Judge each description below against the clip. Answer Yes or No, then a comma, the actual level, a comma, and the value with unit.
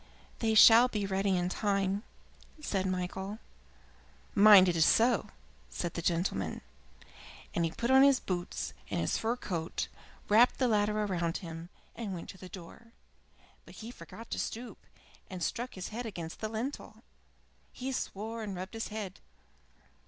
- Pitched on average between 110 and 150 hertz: No, high, 200 Hz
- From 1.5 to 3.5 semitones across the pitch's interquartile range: No, average, 3.9 semitones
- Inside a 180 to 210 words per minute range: No, average, 160 wpm